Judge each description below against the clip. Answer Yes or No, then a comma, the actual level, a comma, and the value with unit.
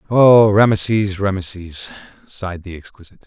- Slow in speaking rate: Yes, slow, 110 wpm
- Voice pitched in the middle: No, low, 100 Hz